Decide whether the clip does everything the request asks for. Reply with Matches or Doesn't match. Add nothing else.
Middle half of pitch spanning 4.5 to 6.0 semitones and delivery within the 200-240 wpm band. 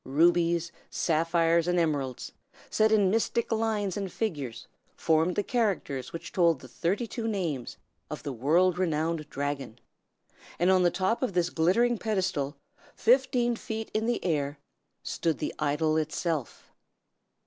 Doesn't match